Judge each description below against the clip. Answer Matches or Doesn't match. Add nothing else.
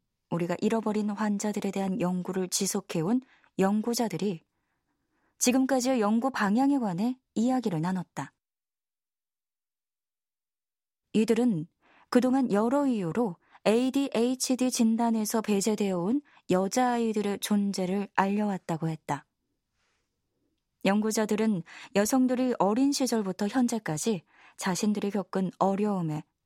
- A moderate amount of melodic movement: Matches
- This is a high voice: Matches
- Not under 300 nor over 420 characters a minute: Doesn't match